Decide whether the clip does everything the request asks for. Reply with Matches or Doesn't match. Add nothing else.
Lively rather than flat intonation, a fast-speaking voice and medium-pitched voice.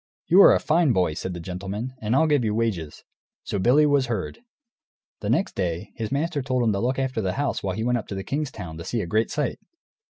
Doesn't match